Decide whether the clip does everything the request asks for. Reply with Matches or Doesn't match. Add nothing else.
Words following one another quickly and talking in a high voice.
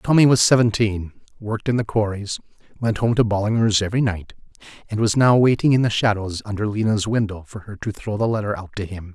Doesn't match